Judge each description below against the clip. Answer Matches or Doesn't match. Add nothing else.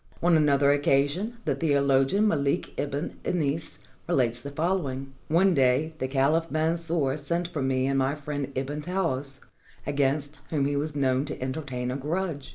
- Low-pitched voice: Doesn't match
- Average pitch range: Matches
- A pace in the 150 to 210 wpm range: Matches